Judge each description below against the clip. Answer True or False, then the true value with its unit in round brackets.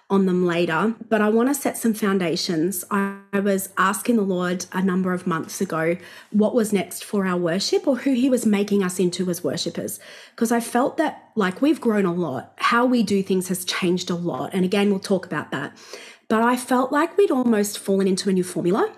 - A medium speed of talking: False (220 wpm)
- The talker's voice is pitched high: True (200 Hz)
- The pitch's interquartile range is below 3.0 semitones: False (4.3 semitones)